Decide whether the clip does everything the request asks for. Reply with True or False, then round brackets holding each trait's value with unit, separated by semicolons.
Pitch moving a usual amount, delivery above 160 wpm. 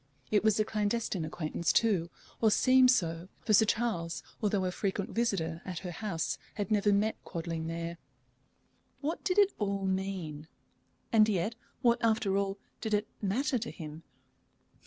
False (4.4 semitones; 155 wpm)